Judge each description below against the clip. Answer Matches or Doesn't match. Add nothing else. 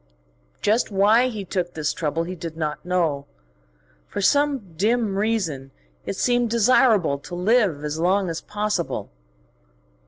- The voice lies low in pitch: Doesn't match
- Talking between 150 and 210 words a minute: Doesn't match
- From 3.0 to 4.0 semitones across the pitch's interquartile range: Doesn't match